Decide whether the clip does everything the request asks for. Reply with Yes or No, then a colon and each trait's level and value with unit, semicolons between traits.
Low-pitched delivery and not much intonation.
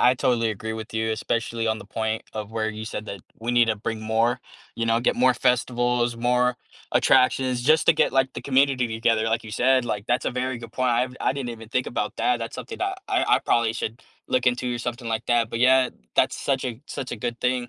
Yes: low, 120 Hz; narrow, 2.0 semitones